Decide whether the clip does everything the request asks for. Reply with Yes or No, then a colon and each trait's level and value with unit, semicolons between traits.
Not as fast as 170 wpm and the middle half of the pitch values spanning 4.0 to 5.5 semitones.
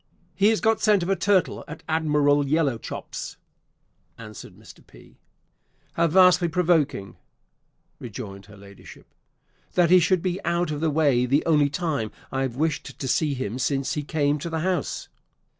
Yes: average, 160 wpm; average, 4.5 semitones